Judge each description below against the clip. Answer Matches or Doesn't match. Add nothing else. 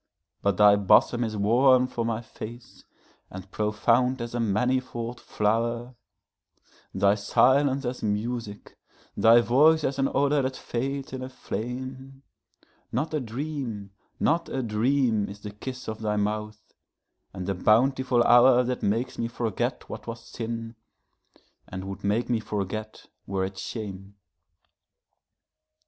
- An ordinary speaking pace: Doesn't match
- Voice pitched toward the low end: Matches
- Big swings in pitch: Doesn't match